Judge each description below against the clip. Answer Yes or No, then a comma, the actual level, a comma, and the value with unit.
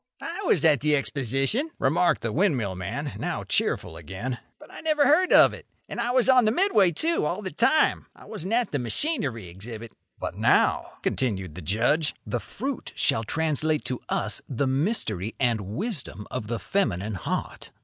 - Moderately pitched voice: Yes, medium, 145 Hz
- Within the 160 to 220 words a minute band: Yes, average, 180 wpm